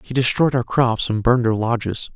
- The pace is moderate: No, fast, 225 wpm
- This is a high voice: No, low, 120 Hz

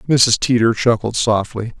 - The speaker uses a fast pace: No, slow, 135 wpm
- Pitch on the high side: No, low, 115 Hz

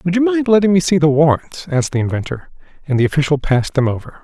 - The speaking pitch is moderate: Yes, medium, 160 Hz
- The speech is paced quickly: Yes, fast, 240 wpm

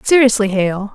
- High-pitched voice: Yes, high, 215 Hz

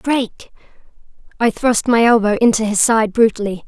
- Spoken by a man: No, female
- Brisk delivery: No, average, 145 wpm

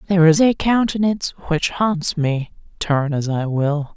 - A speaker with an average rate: Yes, average, 165 wpm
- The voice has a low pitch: No, medium, 170 Hz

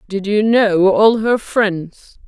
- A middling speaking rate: Yes, average, 160 wpm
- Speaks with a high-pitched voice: Yes, high, 205 Hz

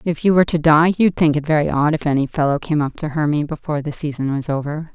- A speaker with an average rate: No, fast, 265 wpm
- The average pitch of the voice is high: No, medium, 150 Hz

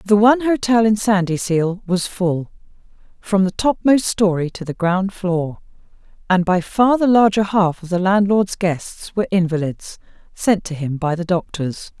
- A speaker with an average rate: Yes, average, 165 wpm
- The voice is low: No, high, 190 Hz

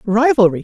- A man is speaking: No, female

